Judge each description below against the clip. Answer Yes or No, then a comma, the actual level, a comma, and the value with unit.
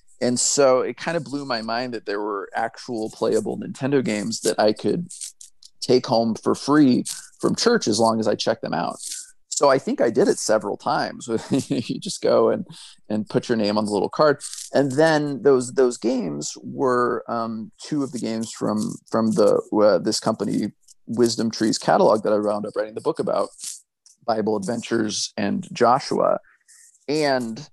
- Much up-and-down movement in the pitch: Yes, wide, 6.3 semitones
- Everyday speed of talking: Yes, average, 180 wpm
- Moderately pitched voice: No, low, 125 Hz